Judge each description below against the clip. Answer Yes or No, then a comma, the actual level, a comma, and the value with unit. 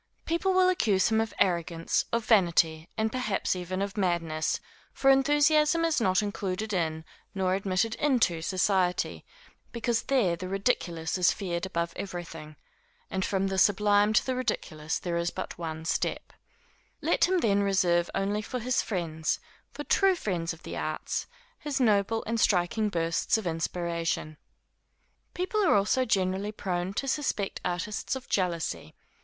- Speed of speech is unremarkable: Yes, average, 150 wpm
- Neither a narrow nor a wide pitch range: Yes, average, 4.7 semitones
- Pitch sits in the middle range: No, high, 195 Hz